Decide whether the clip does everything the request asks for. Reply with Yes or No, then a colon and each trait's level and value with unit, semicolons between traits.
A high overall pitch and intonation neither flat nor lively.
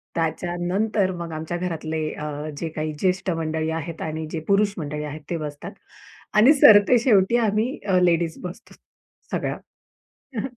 No: medium, 175 Hz; average, 4.1 semitones